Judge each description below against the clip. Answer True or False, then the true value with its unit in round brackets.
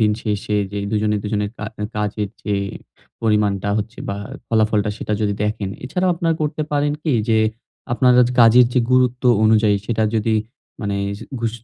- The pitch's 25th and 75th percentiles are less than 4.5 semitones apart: True (2.9 semitones)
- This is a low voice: True (110 Hz)